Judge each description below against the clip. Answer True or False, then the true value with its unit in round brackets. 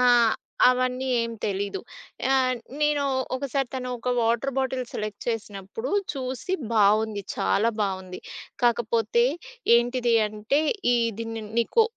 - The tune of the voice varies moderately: True (3.2 semitones)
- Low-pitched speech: False (235 Hz)